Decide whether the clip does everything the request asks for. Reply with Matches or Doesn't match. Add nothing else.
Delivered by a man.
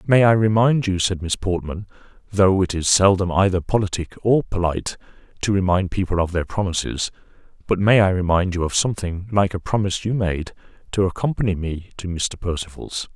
Matches